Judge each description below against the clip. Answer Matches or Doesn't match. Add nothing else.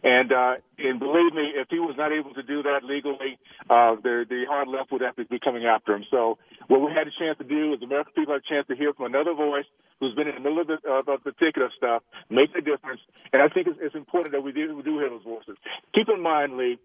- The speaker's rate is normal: Doesn't match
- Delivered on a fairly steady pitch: Doesn't match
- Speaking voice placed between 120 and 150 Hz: Matches